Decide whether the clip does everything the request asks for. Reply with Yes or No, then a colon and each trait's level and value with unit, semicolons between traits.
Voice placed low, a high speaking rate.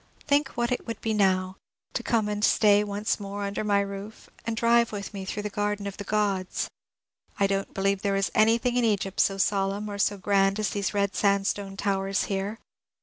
No: high, 200 Hz; fast, 210 wpm